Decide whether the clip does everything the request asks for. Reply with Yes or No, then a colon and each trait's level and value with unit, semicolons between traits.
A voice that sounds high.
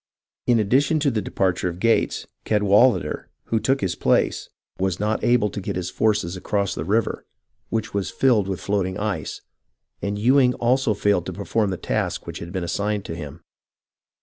No: low, 105 Hz